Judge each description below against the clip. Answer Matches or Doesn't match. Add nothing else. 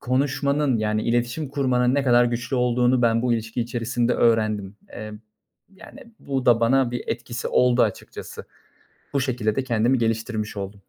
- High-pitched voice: Doesn't match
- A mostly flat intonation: Matches